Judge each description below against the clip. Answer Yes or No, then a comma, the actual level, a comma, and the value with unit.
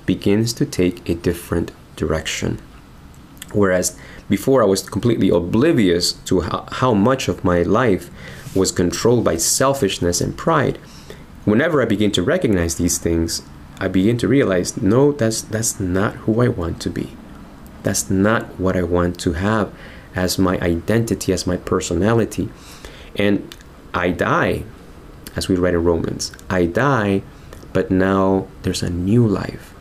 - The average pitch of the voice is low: Yes, very low, 95 Hz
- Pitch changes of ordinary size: Yes, average, 3.0 semitones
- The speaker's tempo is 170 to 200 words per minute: No, average, 145 wpm